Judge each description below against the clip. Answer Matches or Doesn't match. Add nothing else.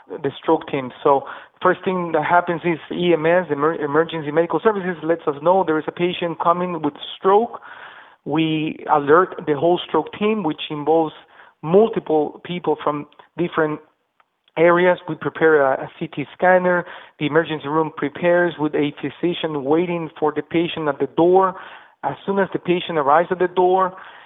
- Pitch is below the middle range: Doesn't match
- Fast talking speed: Doesn't match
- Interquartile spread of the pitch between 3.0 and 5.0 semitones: Doesn't match